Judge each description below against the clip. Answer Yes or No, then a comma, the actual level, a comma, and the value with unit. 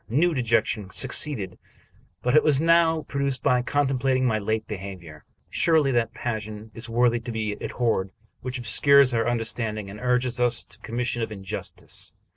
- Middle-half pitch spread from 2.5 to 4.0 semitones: Yes, average, 3.5 semitones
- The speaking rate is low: No, average, 160 wpm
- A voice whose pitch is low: Yes, low, 120 Hz